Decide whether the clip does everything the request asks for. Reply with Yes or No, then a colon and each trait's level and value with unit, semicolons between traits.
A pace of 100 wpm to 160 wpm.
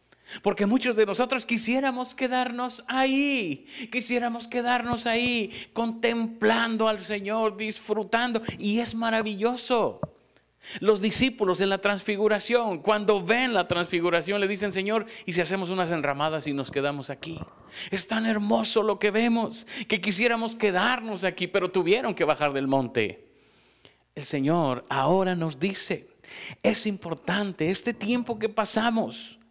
Yes: average, 130 wpm